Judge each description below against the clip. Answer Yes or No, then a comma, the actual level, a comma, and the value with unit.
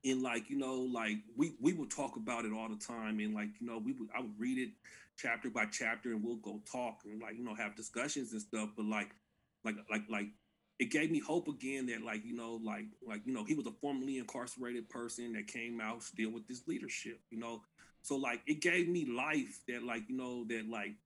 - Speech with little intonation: No, average, 3.0 semitones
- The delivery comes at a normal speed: No, fast, 240 wpm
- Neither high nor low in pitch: No, low, 115 Hz